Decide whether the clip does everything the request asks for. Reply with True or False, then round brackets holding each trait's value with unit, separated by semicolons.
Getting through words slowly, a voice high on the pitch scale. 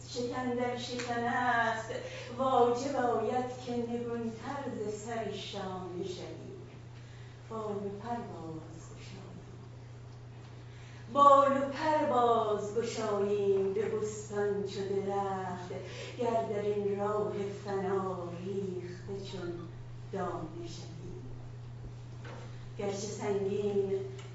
True (85 wpm; 200 Hz)